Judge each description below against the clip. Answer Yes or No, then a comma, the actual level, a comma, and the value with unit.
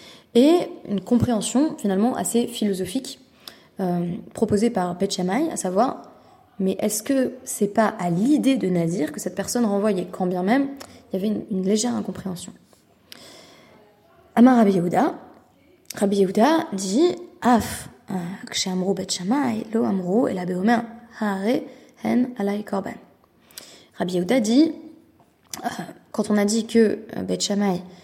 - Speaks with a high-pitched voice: Yes, high, 215 Hz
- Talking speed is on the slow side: Yes, slow, 110 wpm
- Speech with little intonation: No, average, 4.2 semitones